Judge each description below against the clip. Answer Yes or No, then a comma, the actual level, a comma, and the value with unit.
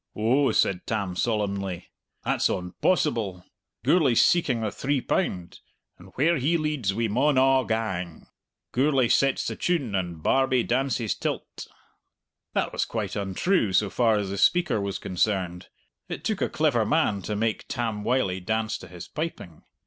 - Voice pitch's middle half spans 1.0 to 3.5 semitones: No, wide, 5.6 semitones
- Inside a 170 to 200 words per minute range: No, average, 155 wpm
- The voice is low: Yes, low, 110 Hz